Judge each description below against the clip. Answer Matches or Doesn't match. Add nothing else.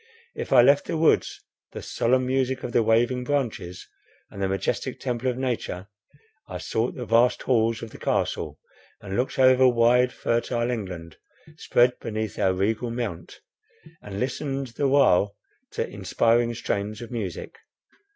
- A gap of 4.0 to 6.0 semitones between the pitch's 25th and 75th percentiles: Doesn't match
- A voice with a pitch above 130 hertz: Doesn't match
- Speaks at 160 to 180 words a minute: Doesn't match